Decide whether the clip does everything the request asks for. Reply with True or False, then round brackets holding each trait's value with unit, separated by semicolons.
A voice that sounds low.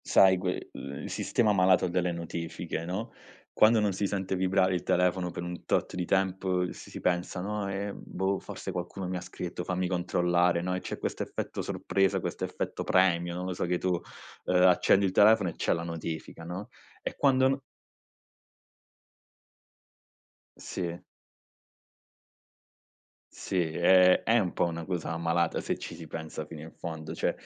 True (90 Hz)